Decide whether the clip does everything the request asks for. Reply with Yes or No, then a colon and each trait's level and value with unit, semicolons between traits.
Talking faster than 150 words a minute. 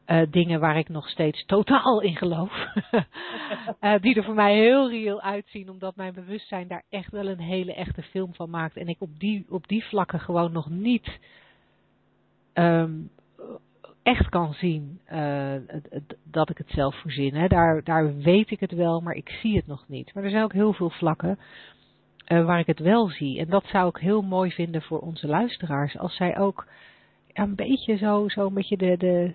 Yes: average, 195 wpm